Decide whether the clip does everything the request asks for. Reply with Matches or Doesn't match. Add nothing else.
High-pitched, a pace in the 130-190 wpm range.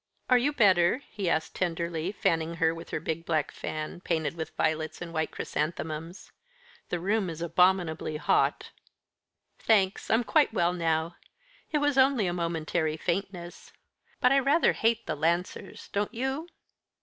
Doesn't match